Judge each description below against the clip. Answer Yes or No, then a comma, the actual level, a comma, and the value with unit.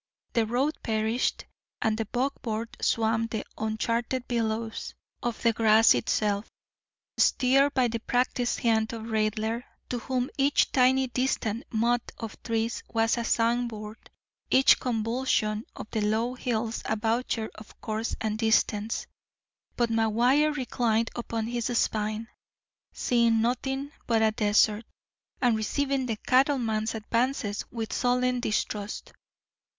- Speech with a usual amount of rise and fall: No, narrow, 2.1 semitones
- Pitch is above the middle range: Yes, high, 230 Hz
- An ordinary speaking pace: No, slow, 125 wpm